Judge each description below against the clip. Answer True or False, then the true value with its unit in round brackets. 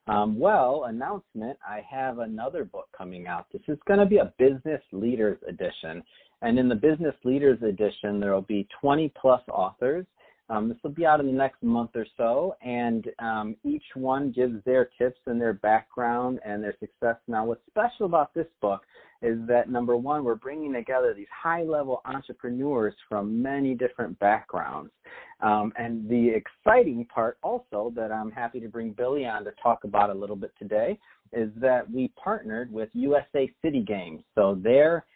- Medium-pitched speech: False (125 Hz)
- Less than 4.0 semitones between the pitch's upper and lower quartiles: False (4.8 semitones)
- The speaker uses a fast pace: False (180 wpm)